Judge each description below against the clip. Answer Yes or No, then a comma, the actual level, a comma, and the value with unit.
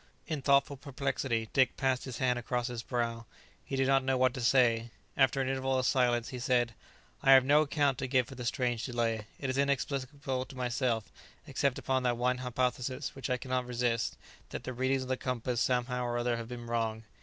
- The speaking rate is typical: No, fast, 210 wpm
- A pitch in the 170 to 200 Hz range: No, low, 125 Hz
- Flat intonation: Yes, narrow, 1.7 semitones